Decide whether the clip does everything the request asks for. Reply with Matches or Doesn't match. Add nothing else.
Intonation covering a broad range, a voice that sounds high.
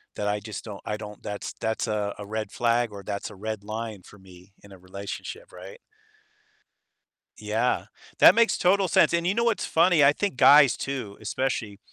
Doesn't match